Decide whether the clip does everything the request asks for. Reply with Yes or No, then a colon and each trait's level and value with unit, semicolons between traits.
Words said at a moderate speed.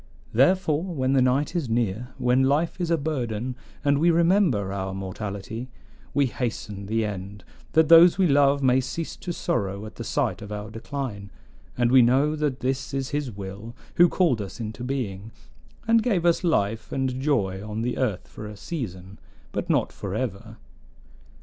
Yes: average, 175 wpm